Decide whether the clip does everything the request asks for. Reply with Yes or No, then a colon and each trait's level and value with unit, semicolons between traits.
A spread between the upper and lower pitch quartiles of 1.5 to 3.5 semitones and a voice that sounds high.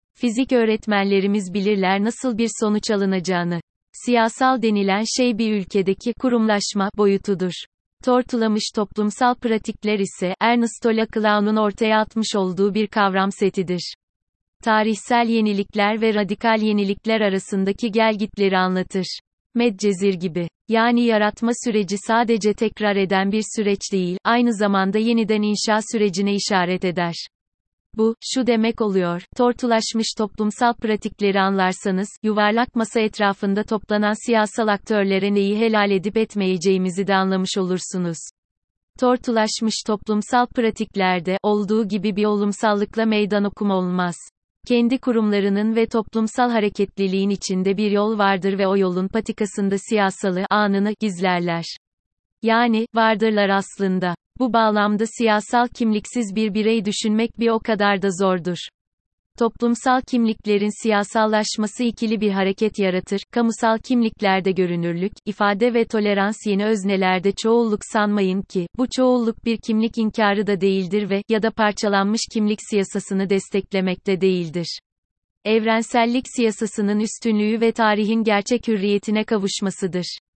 Yes: narrow, 2.4 semitones; high, 210 Hz